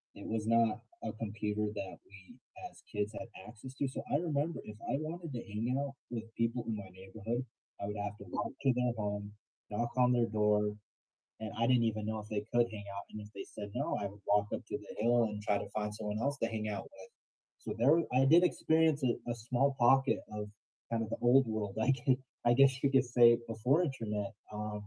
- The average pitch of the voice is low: Yes, low, 115 Hz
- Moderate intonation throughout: Yes, average, 3.3 semitones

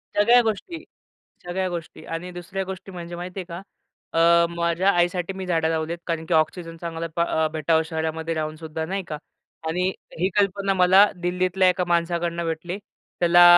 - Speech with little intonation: Yes, narrow, 2.0 semitones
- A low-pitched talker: No, medium, 175 Hz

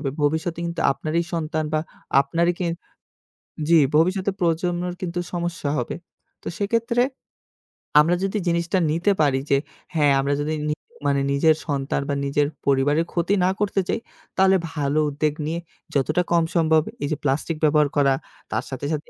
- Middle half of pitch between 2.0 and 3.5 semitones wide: Yes, average, 3.1 semitones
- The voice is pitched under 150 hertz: No, medium, 160 Hz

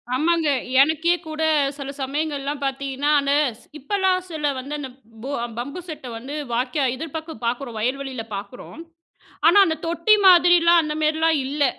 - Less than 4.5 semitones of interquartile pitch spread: Yes, average, 3.2 semitones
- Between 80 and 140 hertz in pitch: No, very high, 295 Hz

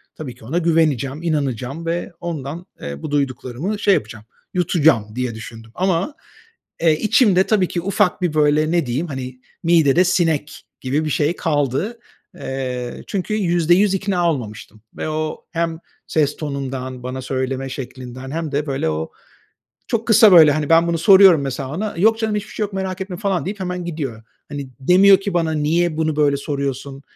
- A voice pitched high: No, medium, 155 Hz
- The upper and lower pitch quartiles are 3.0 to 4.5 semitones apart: No, average, 5.0 semitones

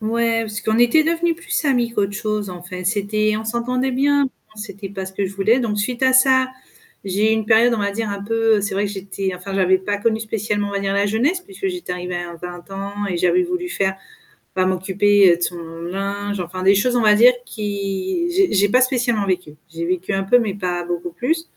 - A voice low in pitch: No, high, 205 Hz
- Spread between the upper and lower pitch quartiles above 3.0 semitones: Yes, average, 3.7 semitones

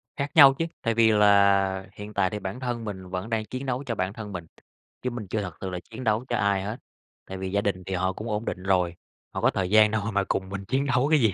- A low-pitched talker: Yes, low, 105 Hz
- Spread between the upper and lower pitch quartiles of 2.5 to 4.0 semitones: Yes, average, 3.4 semitones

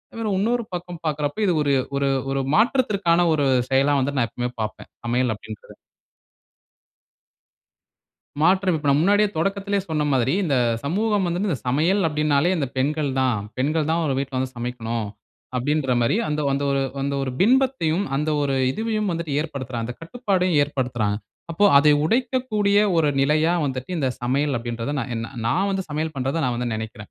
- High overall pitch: No, medium, 150 Hz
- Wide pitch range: Yes, wide, 5.9 semitones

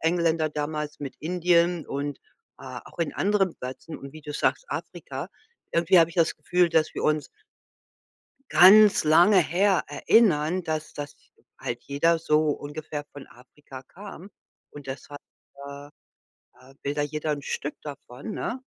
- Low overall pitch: No, medium, 155 Hz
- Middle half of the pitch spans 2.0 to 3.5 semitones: Yes, average, 3.1 semitones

